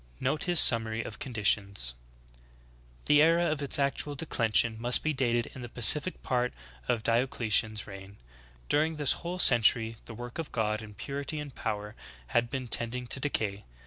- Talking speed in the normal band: Yes, average, 175 wpm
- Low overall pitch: Yes, low, 120 Hz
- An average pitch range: Yes, average, 4.5 semitones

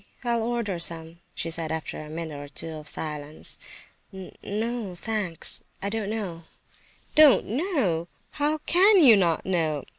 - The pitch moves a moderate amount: No, wide, 6.3 semitones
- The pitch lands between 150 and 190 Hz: Yes, medium, 185 Hz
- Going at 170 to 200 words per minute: No, average, 150 wpm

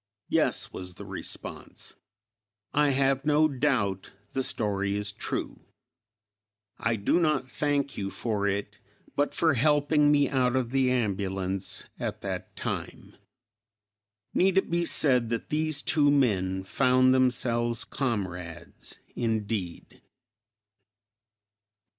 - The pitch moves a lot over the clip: Yes, wide, 6.1 semitones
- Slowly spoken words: Yes, slow, 115 wpm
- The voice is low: Yes, low, 125 Hz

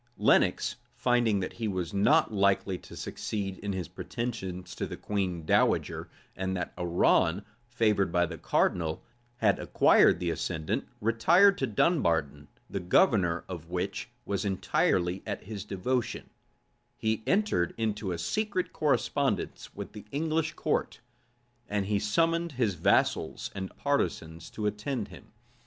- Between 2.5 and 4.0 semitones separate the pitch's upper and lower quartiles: No, average, 5.1 semitones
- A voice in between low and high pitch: No, low, 100 Hz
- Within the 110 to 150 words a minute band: Yes, average, 140 wpm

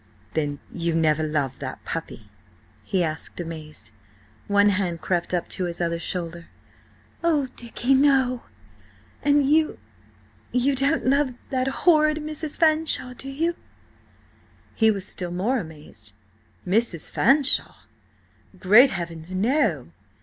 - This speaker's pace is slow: Yes, slow, 120 wpm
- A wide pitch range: Yes, wide, 8.5 semitones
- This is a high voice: Yes, high, 205 Hz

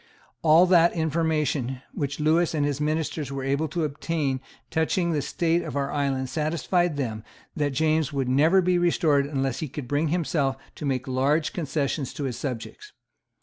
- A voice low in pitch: No, medium, 150 Hz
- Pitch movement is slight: No, average, 3.0 semitones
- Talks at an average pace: Yes, average, 170 wpm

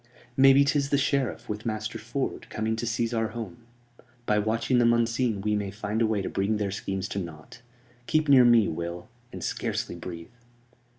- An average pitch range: Yes, average, 3.1 semitones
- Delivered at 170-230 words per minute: Yes, average, 190 wpm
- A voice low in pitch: Yes, low, 110 Hz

